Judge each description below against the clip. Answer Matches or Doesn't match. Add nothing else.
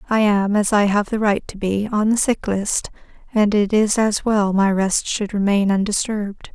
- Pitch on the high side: Matches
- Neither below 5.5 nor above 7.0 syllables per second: Doesn't match